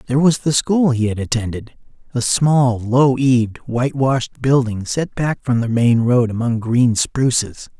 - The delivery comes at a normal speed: Yes, average, 175 wpm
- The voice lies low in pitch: Yes, low, 125 Hz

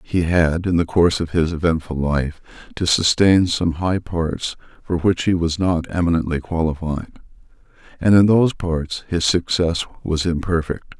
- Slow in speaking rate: No, average, 160 wpm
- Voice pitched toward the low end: Yes, very low, 85 Hz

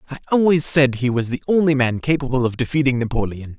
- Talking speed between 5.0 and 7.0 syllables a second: Yes, 6.3 syllables/s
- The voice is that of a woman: No, male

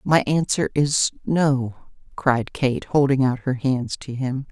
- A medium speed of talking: Yes, average, 160 wpm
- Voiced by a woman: Yes, female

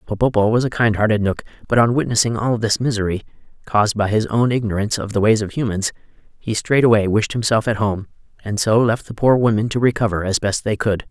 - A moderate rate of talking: No, fast, 215 wpm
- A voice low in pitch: Yes, low, 110 Hz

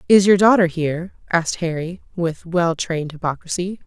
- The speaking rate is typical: Yes, average, 155 wpm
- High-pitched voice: No, medium, 175 Hz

